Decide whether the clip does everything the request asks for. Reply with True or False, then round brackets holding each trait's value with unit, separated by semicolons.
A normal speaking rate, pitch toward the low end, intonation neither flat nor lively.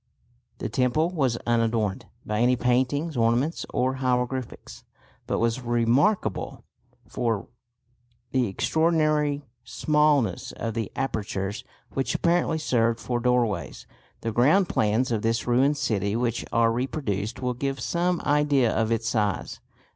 False (125 wpm; 125 Hz; 3.8 semitones)